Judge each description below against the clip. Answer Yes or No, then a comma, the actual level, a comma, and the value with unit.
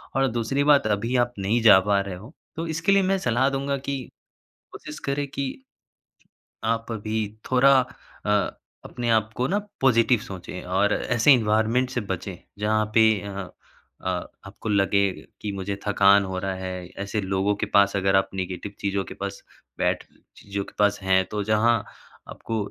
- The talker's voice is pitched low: Yes, low, 105 Hz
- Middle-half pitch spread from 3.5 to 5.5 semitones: Yes, average, 4.2 semitones